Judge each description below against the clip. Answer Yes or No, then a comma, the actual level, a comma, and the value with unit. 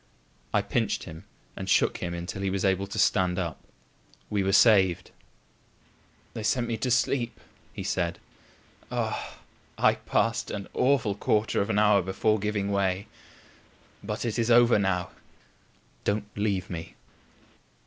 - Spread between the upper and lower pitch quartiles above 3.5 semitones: No, narrow, 2.5 semitones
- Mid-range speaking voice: No, low, 100 Hz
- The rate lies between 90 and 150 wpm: Yes, average, 145 wpm